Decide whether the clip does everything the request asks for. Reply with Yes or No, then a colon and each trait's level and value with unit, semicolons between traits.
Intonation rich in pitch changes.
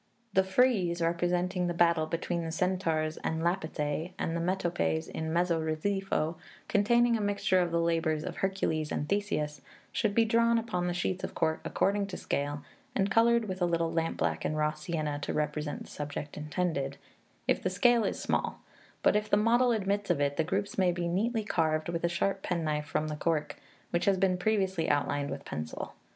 No: average, 3.8 semitones